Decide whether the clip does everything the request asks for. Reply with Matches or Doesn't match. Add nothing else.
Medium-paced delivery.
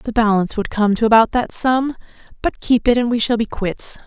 Doesn't match